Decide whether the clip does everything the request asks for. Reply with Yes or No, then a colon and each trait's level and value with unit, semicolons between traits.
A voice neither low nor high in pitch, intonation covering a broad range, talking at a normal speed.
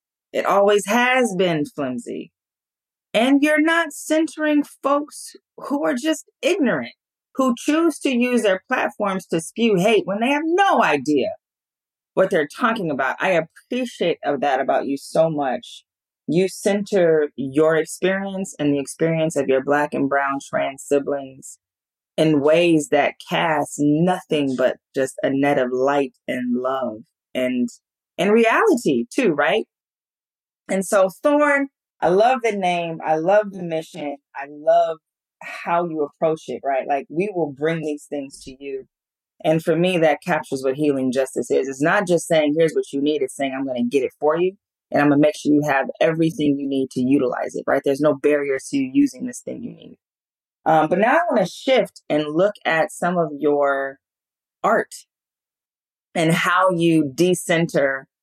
Yes: medium, 160 Hz; wide, 6.5 semitones; average, 170 wpm